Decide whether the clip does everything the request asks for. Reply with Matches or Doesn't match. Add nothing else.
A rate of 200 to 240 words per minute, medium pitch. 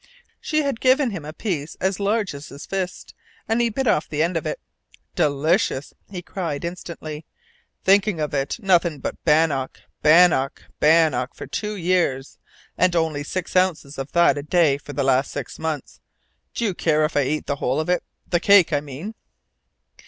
Doesn't match